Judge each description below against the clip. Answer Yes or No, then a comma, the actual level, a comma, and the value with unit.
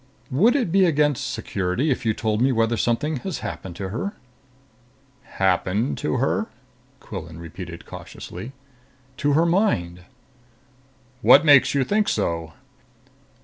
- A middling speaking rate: No, slow, 130 wpm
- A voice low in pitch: Yes, low, 120 Hz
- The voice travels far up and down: Yes, wide, 8.5 semitones